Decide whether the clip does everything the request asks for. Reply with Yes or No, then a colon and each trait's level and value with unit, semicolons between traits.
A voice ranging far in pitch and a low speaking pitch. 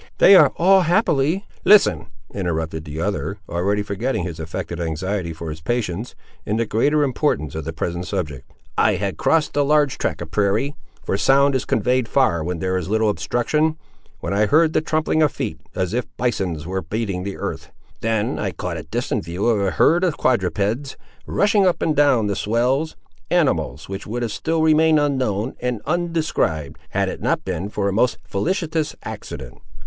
Yes: wide, 8.2 semitones; low, 110 Hz